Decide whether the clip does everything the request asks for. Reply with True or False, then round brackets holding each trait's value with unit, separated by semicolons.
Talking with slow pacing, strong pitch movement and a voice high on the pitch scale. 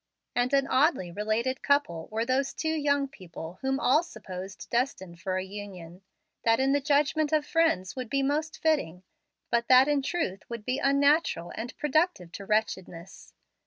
False (165 wpm; 7.0 semitones; 255 Hz)